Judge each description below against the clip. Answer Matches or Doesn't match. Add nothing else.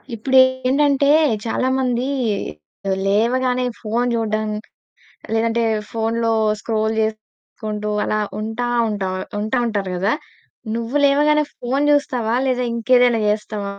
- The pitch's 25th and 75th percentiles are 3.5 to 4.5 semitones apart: Doesn't match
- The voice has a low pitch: Doesn't match